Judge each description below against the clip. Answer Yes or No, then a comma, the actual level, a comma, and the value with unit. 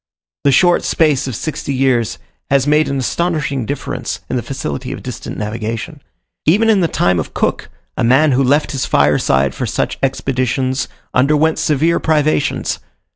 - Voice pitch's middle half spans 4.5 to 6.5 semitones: No, average, 3.6 semitones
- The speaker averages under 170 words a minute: Yes, average, 160 wpm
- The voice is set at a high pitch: No, low, 135 Hz